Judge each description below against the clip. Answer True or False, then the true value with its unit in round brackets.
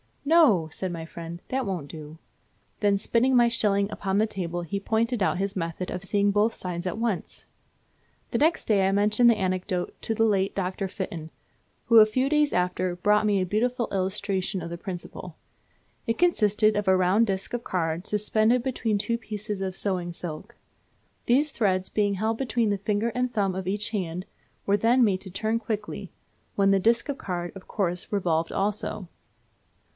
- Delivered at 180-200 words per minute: True (185 wpm)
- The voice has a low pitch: False (200 Hz)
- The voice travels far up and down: False (3.4 semitones)